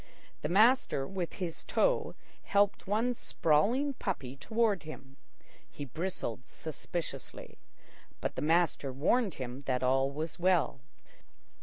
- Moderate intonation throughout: No, wide, 6.9 semitones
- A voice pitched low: No, medium, 165 Hz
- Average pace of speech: No, slow, 120 wpm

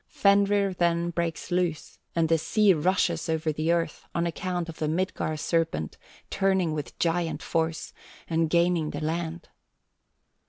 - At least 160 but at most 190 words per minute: No, average, 145 wpm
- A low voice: No, medium, 170 Hz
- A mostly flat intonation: Yes, narrow, 1.8 semitones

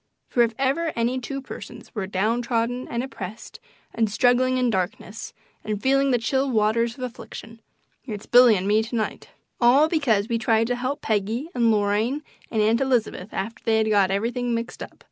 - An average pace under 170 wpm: No, average, 185 wpm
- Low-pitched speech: No, high, 230 Hz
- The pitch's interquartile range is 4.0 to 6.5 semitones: No, average, 2.7 semitones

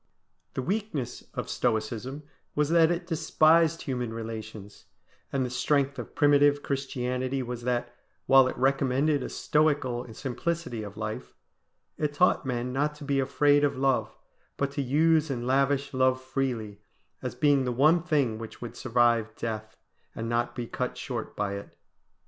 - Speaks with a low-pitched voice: Yes, low, 130 Hz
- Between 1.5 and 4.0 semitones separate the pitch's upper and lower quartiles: Yes, average, 3.3 semitones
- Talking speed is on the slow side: No, average, 155 wpm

